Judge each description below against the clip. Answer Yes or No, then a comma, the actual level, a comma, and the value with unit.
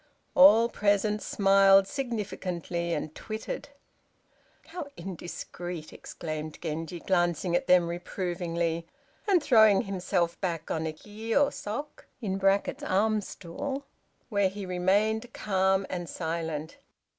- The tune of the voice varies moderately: Yes, average, 3.9 semitones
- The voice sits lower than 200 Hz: Yes, high, 190 Hz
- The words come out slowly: Yes, slow, 105 wpm